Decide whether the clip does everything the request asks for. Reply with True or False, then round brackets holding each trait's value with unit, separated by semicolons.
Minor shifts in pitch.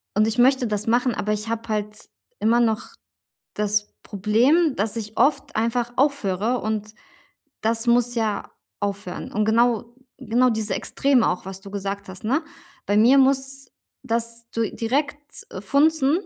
False (3.1 semitones)